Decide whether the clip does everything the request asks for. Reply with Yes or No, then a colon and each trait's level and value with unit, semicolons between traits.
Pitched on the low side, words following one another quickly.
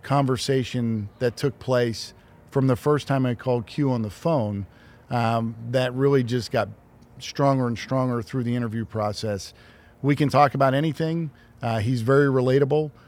No: low, 125 Hz; average, 160 wpm